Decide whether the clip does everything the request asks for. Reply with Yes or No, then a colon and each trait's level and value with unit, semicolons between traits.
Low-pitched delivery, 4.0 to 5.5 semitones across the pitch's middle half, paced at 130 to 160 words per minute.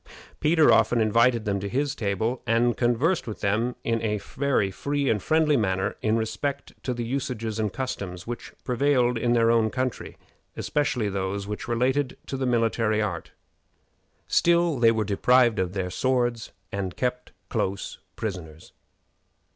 No: low, 115 Hz; average, 3.5 semitones; average, 155 wpm